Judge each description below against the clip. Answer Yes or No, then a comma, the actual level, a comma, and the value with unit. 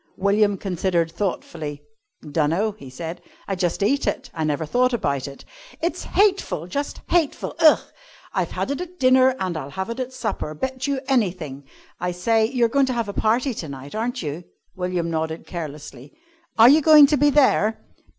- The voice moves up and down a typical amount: No, wide, 8.1 semitones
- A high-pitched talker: Yes, high, 200 Hz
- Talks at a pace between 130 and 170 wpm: No, average, 185 wpm